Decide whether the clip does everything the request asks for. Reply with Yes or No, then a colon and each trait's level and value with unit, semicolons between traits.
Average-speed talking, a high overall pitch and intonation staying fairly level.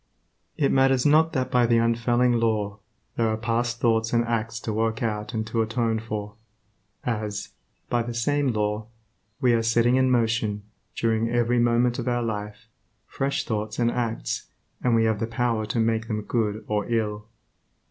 No: average, 175 wpm; low, 115 Hz; narrow, 1.6 semitones